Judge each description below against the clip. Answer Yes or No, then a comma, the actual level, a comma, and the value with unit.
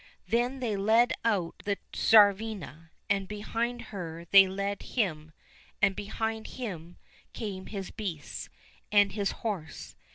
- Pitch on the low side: No, high, 205 Hz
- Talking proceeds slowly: Yes, slow, 125 wpm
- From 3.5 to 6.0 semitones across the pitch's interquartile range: No, average, 2.8 semitones